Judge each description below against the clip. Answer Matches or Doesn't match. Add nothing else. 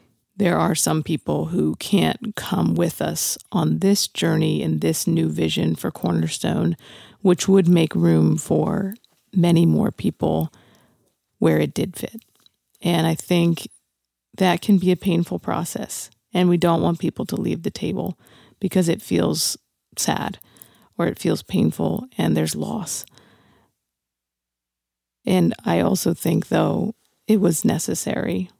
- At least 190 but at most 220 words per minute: Doesn't match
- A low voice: Doesn't match